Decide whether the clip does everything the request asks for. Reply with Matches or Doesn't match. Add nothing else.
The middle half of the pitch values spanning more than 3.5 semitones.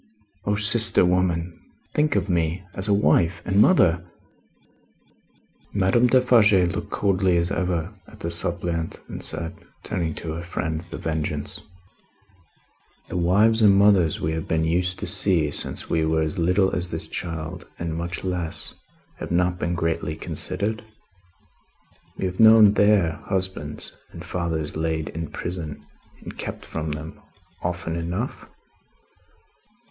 Doesn't match